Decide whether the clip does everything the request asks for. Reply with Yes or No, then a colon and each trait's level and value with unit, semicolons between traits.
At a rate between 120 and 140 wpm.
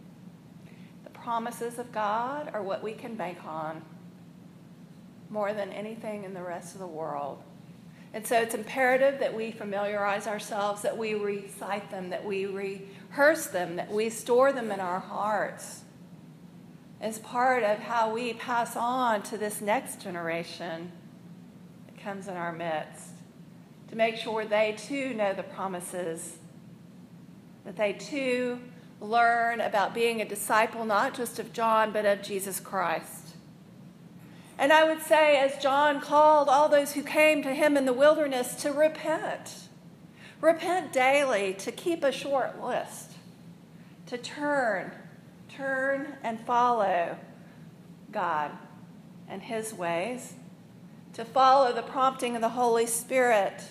Yes: slow, 135 wpm